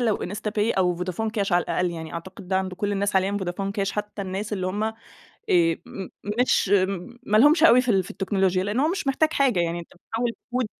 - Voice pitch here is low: No, high, 200 Hz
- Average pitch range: Yes, average, 3.2 semitones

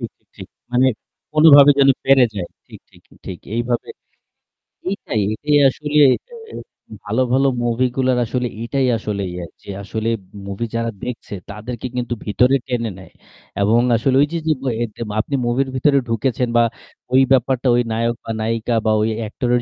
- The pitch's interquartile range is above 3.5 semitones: No, average, 2.8 semitones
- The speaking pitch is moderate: No, low, 120 Hz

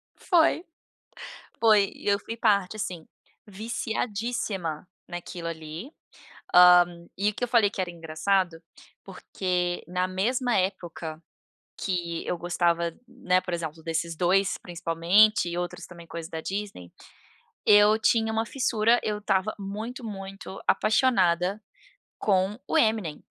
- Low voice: No, high, 190 Hz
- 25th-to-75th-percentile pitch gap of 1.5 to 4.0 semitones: Yes, average, 3.7 semitones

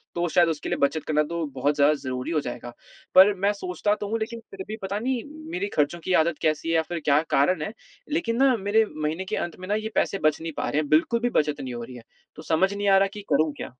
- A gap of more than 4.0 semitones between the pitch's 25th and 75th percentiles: Yes, average, 5.1 semitones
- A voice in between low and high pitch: Yes, medium, 170 Hz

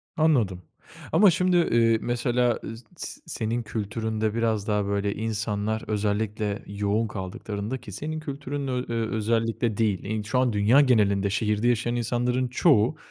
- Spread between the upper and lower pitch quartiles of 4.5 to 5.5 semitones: No, average, 2.7 semitones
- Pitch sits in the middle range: No, low, 110 Hz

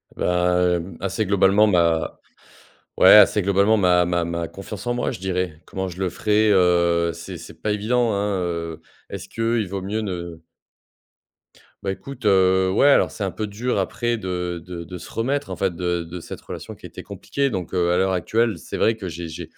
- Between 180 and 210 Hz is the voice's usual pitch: No, very low, 95 Hz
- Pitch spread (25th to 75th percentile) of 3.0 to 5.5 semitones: Yes, average, 3.4 semitones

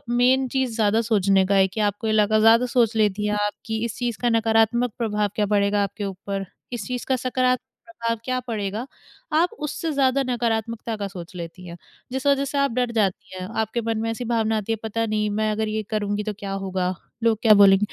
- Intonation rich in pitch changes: No, average, 2.9 semitones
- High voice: Yes, high, 220 Hz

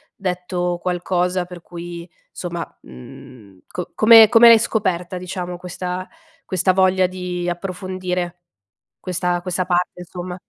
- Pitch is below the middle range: No, medium, 180 Hz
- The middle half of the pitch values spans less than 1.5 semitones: Yes, narrow, 0.9 semitones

